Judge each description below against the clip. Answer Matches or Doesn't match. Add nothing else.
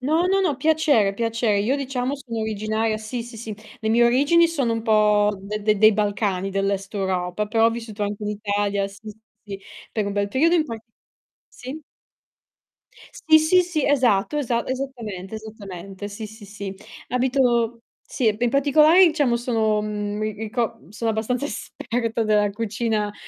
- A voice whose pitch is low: Doesn't match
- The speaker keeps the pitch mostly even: Doesn't match